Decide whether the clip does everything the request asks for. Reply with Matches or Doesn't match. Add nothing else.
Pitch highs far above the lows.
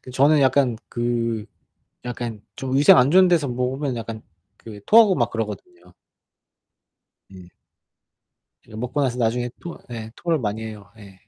Doesn't match